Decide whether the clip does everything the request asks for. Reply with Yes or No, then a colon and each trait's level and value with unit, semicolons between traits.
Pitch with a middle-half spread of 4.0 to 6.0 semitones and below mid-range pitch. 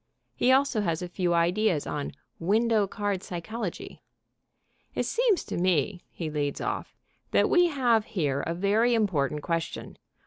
No: average, 5.2 semitones; high, 190 Hz